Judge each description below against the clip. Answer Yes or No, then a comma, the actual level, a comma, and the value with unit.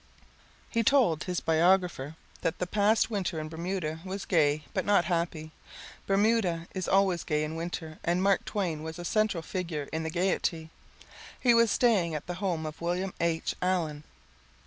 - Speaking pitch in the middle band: Yes, medium, 175 Hz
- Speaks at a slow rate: No, average, 170 wpm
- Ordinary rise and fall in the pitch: Yes, average, 3.3 semitones